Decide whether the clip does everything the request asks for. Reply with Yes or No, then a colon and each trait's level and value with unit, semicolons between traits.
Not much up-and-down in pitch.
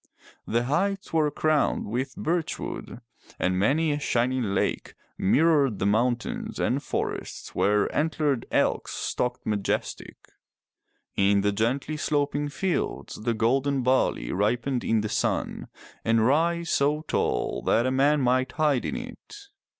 No: average, 5.0 semitones